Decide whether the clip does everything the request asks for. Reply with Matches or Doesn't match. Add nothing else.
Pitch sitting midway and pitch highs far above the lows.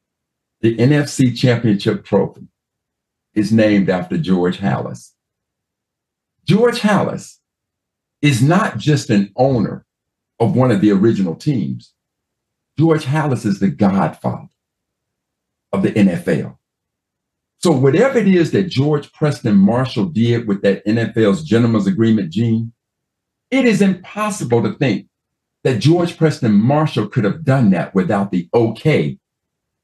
Doesn't match